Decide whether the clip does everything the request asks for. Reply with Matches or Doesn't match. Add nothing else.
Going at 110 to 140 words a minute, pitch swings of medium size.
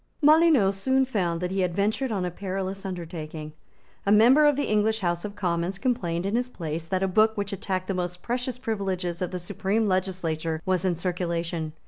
Doesn't match